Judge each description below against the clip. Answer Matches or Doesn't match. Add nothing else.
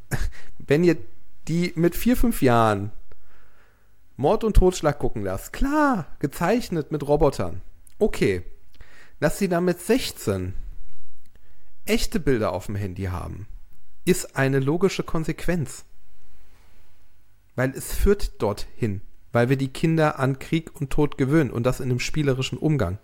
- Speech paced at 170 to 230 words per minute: Doesn't match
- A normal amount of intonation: Doesn't match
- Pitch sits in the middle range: Doesn't match